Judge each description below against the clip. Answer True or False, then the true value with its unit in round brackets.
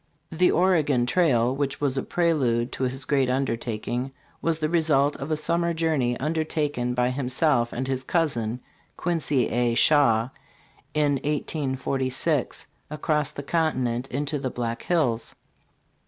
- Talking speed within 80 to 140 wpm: True (135 wpm)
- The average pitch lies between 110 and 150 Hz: True (135 Hz)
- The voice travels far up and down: False (3.9 semitones)